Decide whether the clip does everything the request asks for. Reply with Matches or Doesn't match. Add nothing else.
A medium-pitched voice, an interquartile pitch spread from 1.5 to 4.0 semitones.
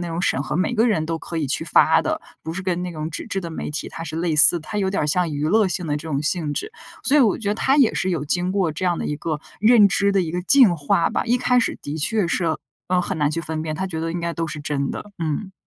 Matches